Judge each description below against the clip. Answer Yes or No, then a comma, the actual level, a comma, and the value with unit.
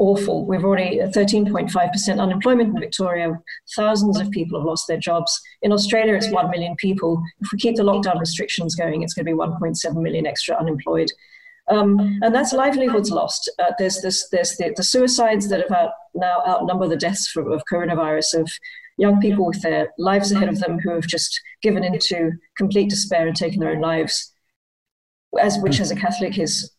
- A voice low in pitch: No, medium, 185 Hz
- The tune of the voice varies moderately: Yes, average, 3.7 semitones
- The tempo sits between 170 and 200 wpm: Yes, average, 190 wpm